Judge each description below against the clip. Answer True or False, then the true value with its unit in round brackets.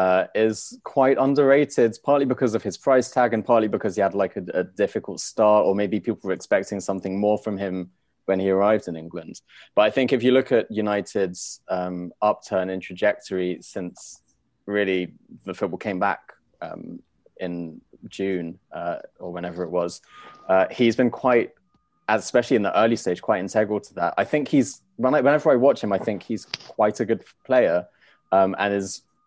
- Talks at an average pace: True (185 wpm)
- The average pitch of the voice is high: False (105 Hz)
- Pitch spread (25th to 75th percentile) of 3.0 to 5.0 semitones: True (4.1 semitones)